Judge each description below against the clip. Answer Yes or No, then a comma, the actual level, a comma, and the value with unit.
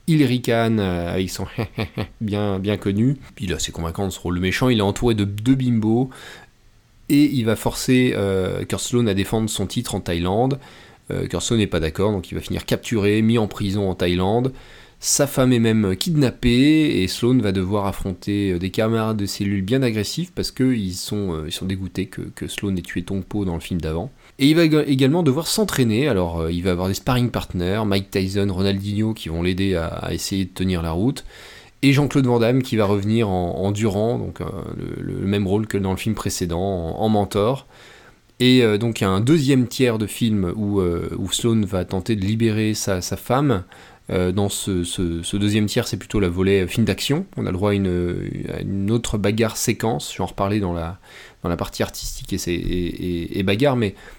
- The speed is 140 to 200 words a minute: No, average, 215 wpm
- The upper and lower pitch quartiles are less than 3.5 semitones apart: No, average, 4.1 semitones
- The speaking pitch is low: Yes, low, 105 Hz